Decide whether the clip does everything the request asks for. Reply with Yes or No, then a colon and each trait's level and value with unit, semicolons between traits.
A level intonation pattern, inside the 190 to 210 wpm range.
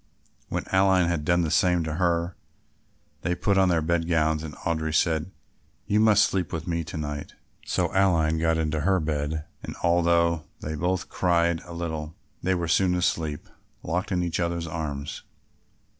No: narrow, 2.1 semitones; average, 175 wpm